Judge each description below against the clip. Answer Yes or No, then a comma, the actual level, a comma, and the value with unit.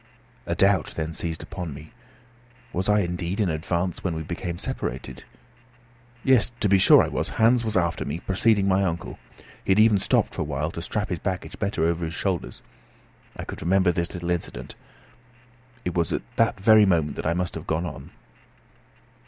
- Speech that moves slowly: No, average, 190 wpm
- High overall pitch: No, very low, 90 Hz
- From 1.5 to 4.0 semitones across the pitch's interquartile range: Yes, average, 2.9 semitones